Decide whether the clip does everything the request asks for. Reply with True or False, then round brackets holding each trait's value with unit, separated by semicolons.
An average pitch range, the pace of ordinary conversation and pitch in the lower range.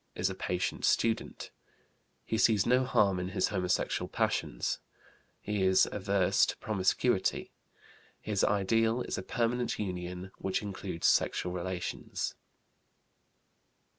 False (3.2 semitones; 115 wpm; 95 Hz)